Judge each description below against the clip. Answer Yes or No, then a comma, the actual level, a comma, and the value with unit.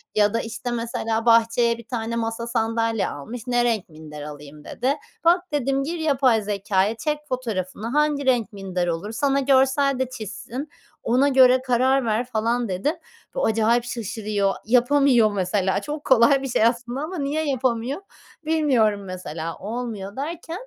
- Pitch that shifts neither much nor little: Yes, average, 4.0 semitones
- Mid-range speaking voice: No, high, 235 Hz